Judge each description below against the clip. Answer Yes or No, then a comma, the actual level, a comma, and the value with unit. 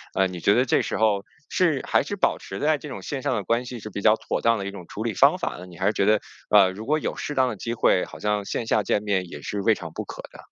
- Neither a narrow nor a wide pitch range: Yes, average, 3.8 semitones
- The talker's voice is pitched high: No, low, 110 Hz